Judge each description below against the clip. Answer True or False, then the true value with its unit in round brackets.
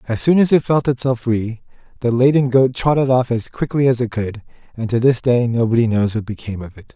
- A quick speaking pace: True (235 wpm)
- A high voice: False (120 Hz)